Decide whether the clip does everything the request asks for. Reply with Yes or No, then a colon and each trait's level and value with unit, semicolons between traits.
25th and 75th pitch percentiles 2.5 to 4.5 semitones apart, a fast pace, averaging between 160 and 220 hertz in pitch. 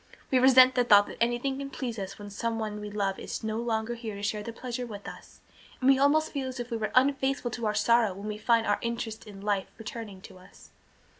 No: average, 3.2 semitones; fast, 240 wpm; high, 230 Hz